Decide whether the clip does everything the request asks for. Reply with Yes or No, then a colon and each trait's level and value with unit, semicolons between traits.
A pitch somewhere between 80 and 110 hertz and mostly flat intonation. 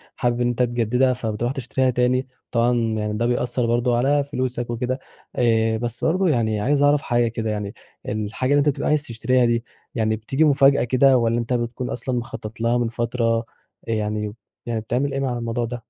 No: low, 120 Hz; narrow, 2.0 semitones